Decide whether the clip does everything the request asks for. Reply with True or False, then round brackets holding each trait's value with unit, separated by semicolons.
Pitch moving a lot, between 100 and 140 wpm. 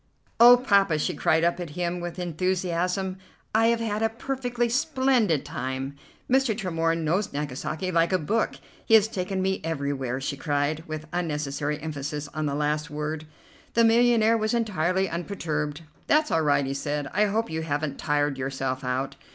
False (6.2 semitones; 165 wpm)